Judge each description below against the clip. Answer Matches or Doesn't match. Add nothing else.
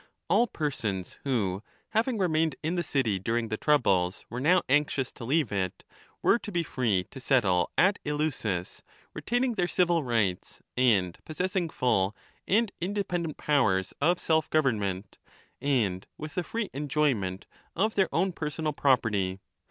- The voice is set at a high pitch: Doesn't match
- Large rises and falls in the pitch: Matches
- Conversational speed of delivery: Matches